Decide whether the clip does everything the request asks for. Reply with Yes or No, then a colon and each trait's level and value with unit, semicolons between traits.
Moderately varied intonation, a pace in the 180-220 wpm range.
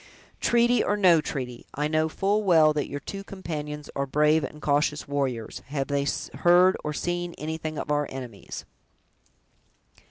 No: average, 3.5 semitones; average, 155 wpm